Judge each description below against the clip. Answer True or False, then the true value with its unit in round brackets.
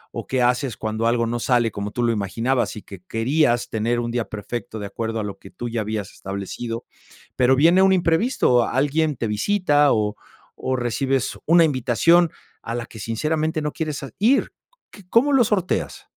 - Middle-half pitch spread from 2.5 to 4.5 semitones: False (5.4 semitones)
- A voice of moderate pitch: False (120 Hz)